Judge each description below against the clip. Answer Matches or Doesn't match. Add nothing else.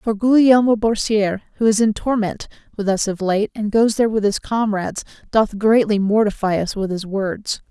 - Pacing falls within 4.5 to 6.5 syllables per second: Matches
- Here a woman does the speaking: Matches